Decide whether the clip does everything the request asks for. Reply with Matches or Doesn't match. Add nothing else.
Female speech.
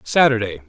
Doesn't match